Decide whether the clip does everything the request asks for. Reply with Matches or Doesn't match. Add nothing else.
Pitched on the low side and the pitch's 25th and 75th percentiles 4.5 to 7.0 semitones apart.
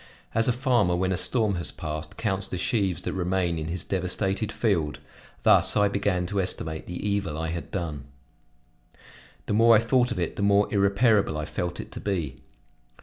Doesn't match